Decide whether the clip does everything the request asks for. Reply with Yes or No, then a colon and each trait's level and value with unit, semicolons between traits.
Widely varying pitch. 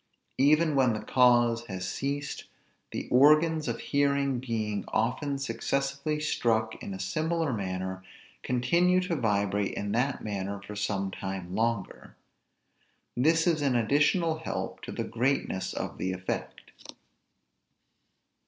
Yes: wide, 5.8 semitones